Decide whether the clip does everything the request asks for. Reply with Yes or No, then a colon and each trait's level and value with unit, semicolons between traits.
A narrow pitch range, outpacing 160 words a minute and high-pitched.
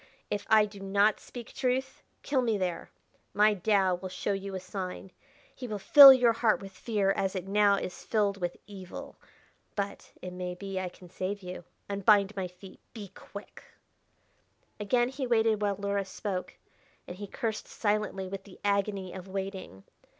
Yes: narrow, 2.1 semitones; average, 170 wpm; high, 200 Hz